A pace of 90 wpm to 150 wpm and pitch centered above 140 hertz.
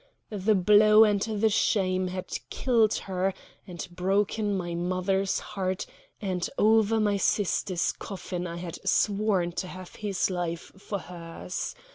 Yes: slow, 135 wpm; high, 190 Hz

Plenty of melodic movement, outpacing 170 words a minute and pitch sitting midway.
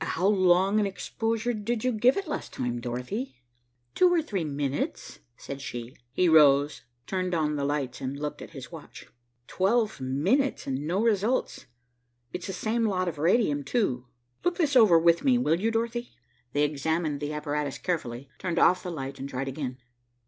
Yes: wide, 7.5 semitones; average, 180 wpm; medium, 170 Hz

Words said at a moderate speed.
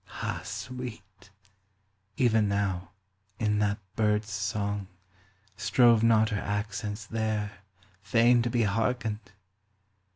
No: slow, 100 wpm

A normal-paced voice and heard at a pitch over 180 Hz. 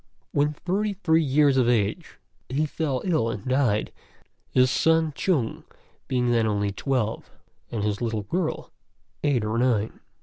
No: average, 145 wpm; low, 130 Hz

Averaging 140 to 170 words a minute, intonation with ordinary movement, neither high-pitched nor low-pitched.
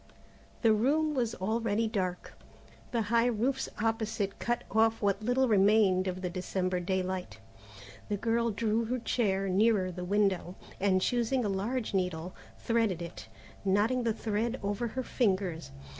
No: average, 145 wpm; average, 3.6 semitones; high, 210 Hz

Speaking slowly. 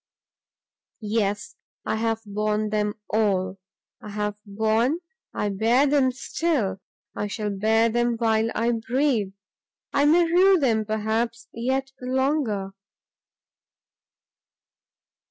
Yes: slow, 100 wpm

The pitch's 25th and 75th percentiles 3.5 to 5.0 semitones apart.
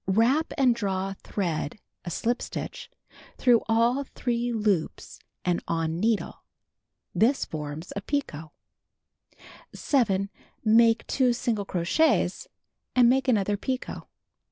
Yes: average, 4.6 semitones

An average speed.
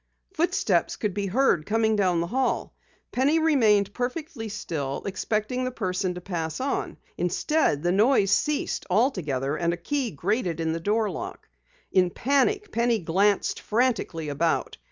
Yes: average, 150 wpm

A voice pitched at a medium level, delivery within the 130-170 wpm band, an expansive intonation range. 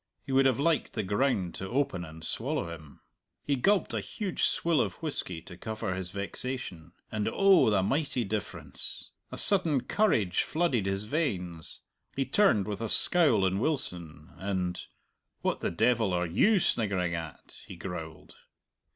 No: low, 105 Hz; average, 160 wpm; wide, 7.7 semitones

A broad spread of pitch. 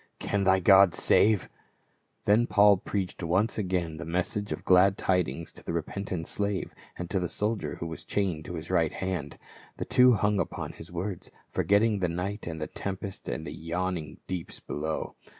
No: average, 3.3 semitones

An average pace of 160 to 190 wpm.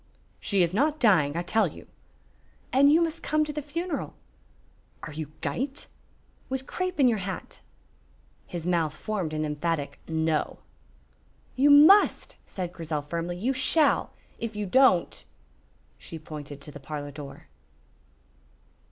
No: average, 145 wpm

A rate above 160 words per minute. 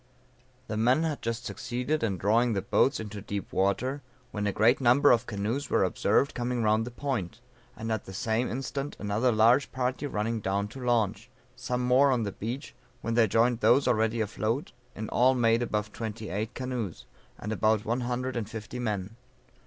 Yes: average, 185 wpm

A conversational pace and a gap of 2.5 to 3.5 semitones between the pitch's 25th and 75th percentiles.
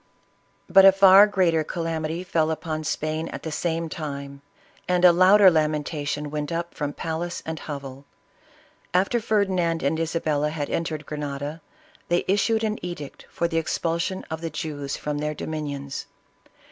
Yes: average, 155 wpm; average, 2.8 semitones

